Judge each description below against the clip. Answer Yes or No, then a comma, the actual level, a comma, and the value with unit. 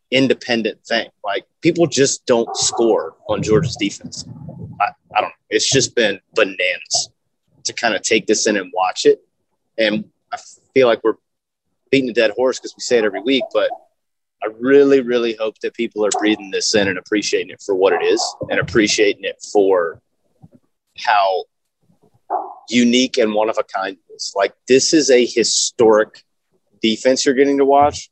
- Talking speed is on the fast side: No, average, 175 wpm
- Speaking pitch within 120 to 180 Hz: Yes, medium, 140 Hz